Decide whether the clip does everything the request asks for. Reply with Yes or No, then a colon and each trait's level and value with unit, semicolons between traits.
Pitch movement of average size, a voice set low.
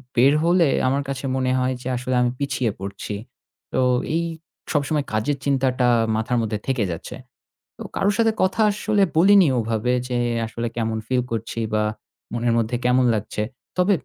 Yes: average, 4.1 semitones; low, 125 Hz